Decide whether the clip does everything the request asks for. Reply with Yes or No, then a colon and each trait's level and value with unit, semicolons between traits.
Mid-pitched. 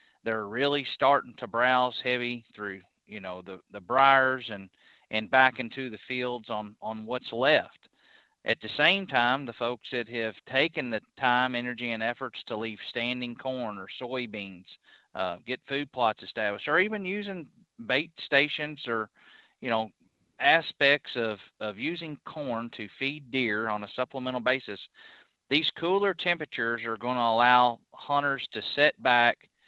No: low, 125 Hz